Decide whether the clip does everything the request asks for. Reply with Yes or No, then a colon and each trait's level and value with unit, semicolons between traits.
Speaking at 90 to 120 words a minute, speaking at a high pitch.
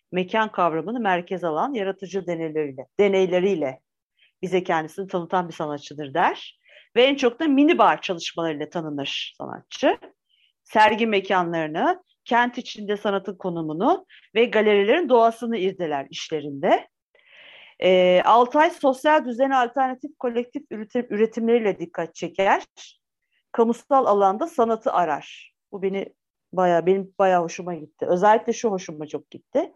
Yes: average, 115 wpm; high, 195 Hz